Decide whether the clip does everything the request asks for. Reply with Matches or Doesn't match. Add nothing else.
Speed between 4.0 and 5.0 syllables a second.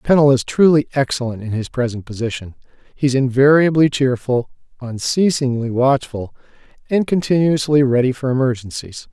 Doesn't match